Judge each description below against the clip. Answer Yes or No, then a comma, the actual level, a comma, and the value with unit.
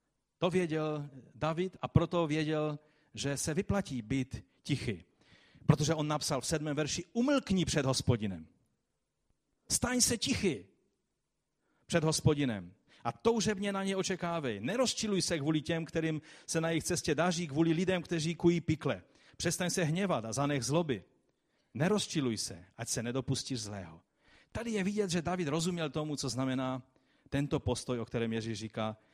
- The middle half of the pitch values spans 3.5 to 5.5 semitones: Yes, average, 5.1 semitones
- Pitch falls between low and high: Yes, medium, 155 Hz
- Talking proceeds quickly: No, average, 150 wpm